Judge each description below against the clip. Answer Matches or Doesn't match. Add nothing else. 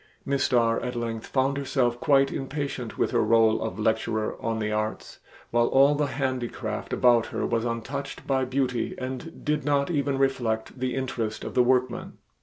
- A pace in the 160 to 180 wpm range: Matches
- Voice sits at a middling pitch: Doesn't match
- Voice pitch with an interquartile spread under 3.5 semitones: Matches